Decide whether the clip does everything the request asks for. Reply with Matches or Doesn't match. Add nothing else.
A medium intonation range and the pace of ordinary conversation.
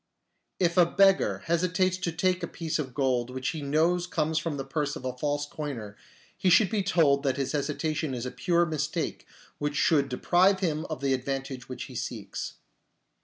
Matches